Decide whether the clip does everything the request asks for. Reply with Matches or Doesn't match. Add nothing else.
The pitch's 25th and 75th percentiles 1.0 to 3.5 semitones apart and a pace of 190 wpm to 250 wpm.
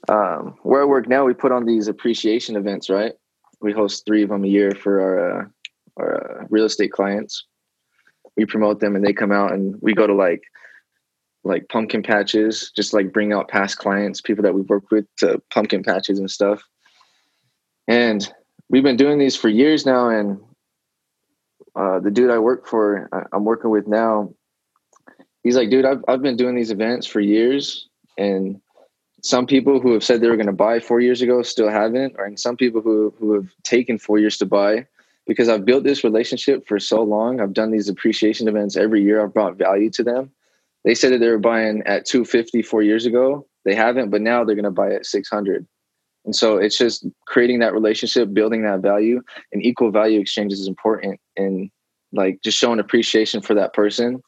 Matches